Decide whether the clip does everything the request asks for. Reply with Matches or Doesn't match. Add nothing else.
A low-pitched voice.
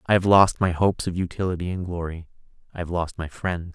Matches